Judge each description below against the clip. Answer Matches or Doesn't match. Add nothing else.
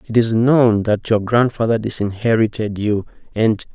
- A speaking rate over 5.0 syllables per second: Doesn't match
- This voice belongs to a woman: Doesn't match